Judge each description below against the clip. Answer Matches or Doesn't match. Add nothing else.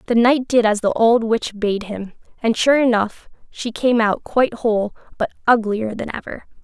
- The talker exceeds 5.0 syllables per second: Doesn't match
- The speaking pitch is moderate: Doesn't match